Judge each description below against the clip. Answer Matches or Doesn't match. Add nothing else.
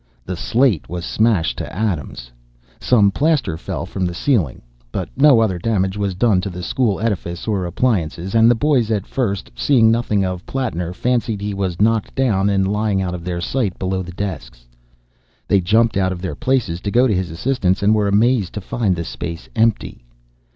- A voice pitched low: Matches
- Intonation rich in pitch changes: Doesn't match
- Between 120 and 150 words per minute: Doesn't match